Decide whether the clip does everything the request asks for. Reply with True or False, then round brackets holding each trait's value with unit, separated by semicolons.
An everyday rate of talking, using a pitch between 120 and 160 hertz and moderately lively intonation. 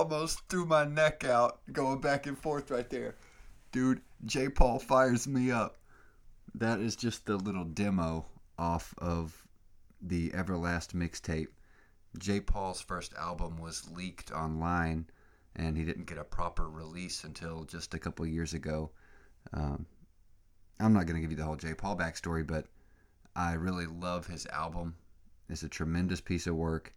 False (160 wpm; 85 Hz; 3.8 semitones)